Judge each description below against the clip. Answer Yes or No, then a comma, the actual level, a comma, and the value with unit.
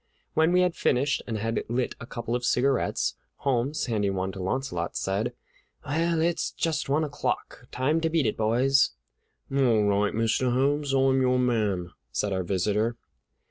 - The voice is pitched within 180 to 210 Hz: No, low, 125 Hz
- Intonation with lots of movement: No, average, 4.7 semitones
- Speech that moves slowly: No, average, 165 wpm